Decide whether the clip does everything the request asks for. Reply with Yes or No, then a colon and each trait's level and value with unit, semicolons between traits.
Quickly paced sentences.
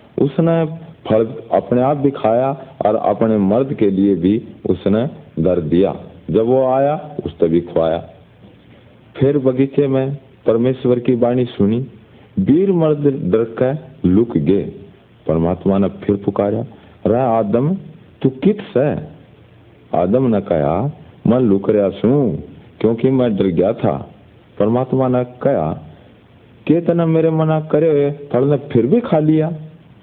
No: average, 140 wpm